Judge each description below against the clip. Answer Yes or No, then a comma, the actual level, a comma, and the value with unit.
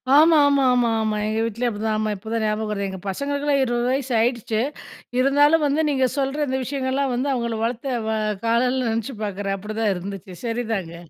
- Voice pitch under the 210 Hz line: No, high, 235 Hz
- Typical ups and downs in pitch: Yes, average, 4.0 semitones